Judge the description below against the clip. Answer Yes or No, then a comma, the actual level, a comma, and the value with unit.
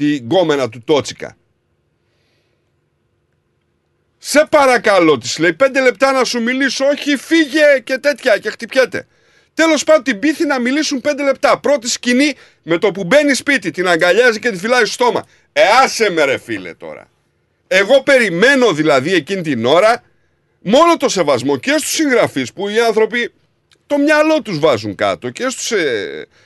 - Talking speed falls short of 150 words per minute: No, average, 160 wpm